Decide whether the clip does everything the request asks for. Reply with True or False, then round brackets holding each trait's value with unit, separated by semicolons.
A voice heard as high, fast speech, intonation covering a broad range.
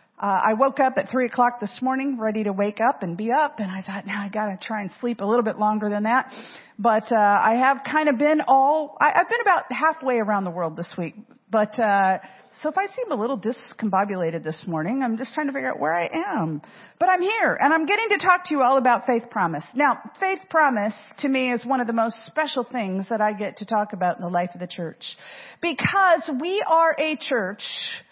True (235 Hz; 235 wpm; 5.8 semitones)